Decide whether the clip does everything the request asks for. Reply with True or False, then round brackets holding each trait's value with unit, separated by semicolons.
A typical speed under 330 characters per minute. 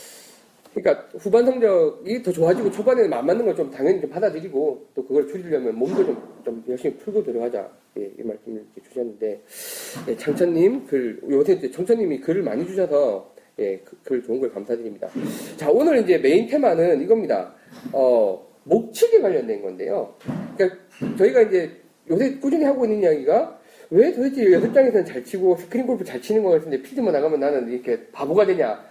False (370 characters per minute)